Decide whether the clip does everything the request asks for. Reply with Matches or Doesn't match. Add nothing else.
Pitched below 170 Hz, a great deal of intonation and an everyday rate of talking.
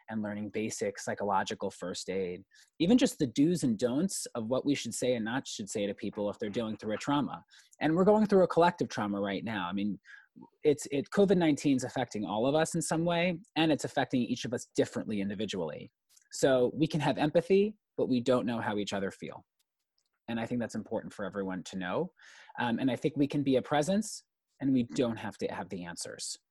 Doesn't match